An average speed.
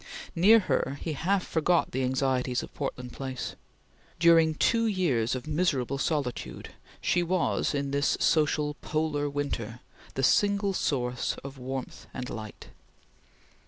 No: slow, 130 wpm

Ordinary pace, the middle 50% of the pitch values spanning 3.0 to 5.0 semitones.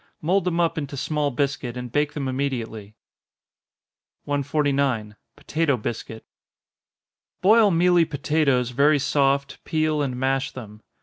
No: slow, 120 wpm; average, 3.3 semitones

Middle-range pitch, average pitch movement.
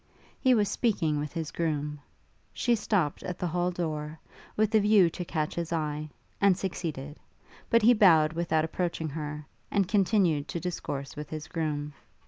Yes: medium, 165 Hz; average, 4.1 semitones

